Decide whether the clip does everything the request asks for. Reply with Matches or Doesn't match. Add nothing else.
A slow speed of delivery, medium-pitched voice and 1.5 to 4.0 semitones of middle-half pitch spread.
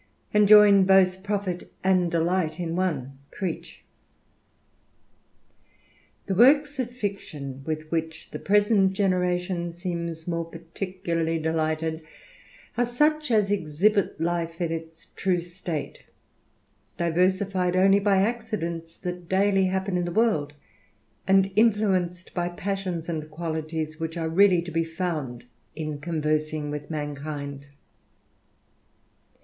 Matches